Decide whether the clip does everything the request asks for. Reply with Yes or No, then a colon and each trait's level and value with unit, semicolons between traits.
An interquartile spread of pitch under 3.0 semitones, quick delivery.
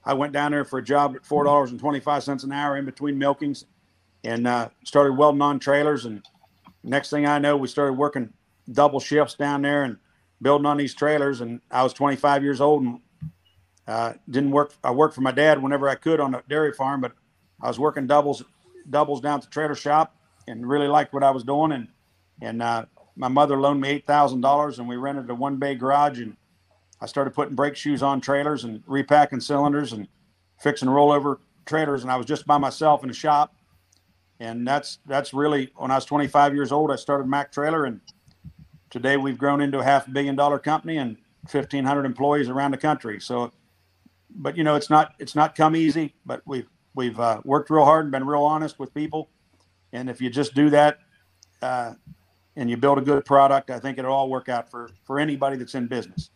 Yes: narrow, 2.5 semitones; fast, 210 wpm